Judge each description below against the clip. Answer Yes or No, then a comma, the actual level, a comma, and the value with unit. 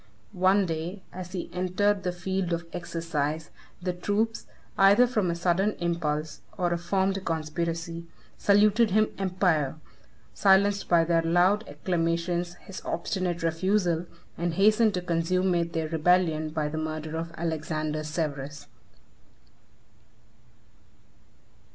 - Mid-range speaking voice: Yes, medium, 175 Hz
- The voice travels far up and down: No, average, 2.7 semitones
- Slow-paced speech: Yes, slow, 120 wpm